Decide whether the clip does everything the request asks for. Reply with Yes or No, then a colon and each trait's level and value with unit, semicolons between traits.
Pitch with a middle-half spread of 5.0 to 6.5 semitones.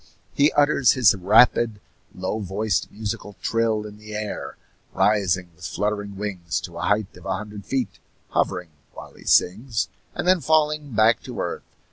No: average, 2.9 semitones